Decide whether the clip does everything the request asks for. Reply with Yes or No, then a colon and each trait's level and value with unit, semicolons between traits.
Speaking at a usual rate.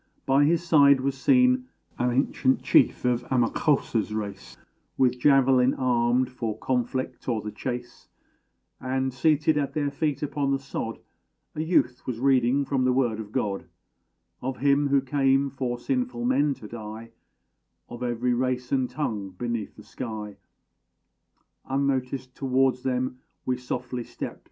Yes: average, 145 wpm